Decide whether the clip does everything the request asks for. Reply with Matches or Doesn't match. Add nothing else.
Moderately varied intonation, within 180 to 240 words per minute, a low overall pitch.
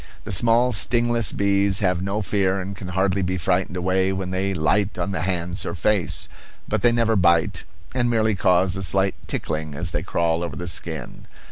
Doesn't match